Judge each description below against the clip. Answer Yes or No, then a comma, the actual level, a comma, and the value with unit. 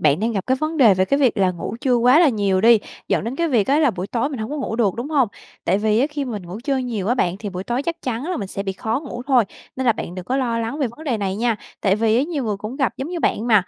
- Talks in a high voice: Yes, high, 235 Hz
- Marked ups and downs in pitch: No, average, 4.8 semitones